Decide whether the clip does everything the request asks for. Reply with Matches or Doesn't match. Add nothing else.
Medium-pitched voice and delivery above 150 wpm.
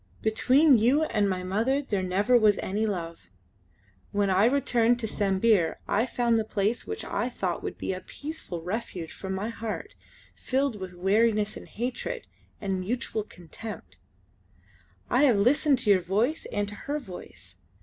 Doesn't match